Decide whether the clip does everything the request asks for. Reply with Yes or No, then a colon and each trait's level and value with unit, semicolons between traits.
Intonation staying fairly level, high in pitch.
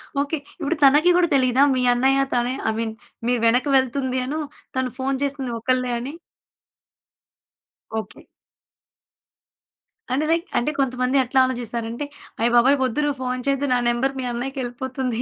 Yes: narrow, 2.0 semitones; very high, 260 Hz